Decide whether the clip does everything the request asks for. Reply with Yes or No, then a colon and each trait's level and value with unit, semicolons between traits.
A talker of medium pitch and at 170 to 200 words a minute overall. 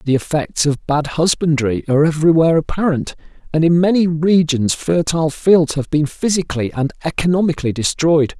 No: medium, 155 Hz; average, 145 wpm